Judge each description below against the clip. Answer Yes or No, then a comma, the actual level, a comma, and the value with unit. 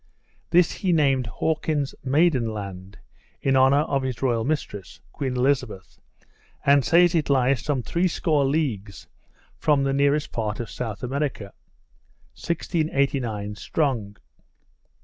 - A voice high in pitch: No, low, 135 Hz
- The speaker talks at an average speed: No, slow, 120 wpm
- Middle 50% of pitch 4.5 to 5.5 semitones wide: Yes, average, 4.9 semitones